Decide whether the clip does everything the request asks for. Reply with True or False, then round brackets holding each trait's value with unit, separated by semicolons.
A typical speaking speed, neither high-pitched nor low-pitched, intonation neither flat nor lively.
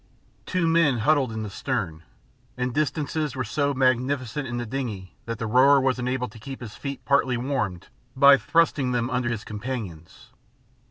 False (170 wpm; 125 Hz; 3.6 semitones)